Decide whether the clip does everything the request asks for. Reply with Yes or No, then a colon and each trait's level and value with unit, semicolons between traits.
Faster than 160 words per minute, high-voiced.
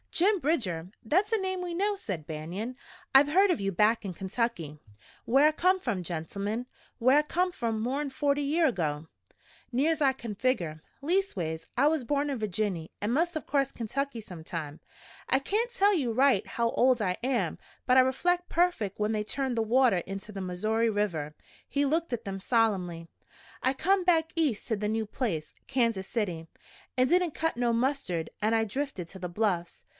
Yes: average, 185 wpm; high, 235 Hz